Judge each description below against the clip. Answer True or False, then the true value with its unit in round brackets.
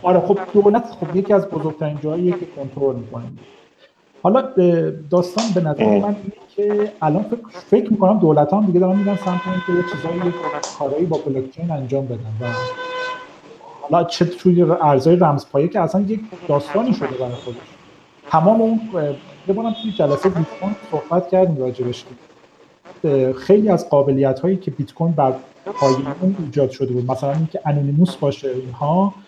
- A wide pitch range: True (5.7 semitones)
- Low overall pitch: False (175 Hz)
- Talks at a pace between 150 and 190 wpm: True (155 wpm)